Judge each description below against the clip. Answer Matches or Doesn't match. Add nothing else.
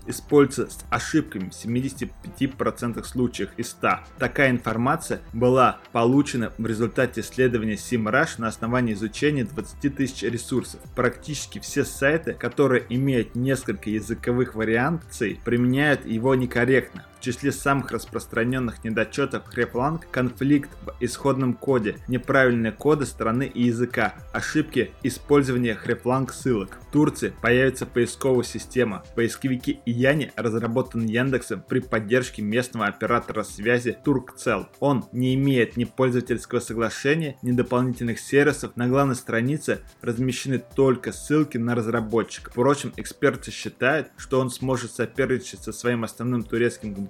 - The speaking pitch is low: Matches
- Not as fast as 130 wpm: Matches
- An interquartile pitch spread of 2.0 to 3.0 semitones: Matches